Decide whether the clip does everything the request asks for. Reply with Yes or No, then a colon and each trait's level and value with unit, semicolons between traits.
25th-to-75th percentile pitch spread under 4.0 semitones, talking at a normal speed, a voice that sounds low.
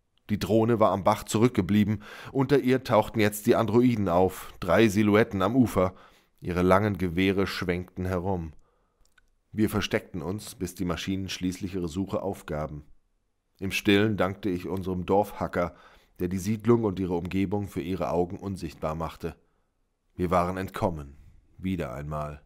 Yes: average, 2.9 semitones; average, 145 wpm; very low, 95 Hz